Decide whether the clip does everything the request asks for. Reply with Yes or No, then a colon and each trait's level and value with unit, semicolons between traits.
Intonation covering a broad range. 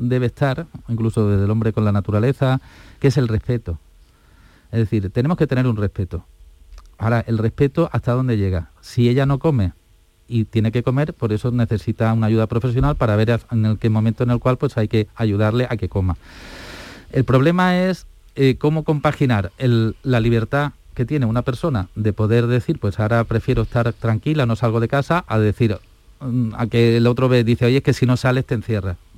No: average, 3.1 semitones